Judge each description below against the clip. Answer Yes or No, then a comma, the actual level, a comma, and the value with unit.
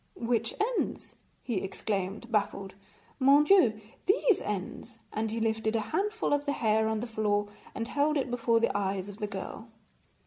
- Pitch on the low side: No, high, 225 Hz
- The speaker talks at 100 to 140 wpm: No, average, 170 wpm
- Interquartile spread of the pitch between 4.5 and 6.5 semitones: No, average, 3.7 semitones